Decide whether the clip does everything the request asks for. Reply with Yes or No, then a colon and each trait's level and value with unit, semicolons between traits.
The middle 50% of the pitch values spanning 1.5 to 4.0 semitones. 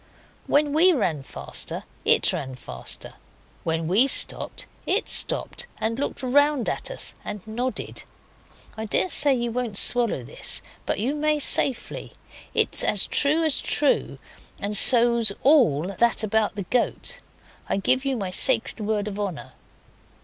No: average, 5.2 semitones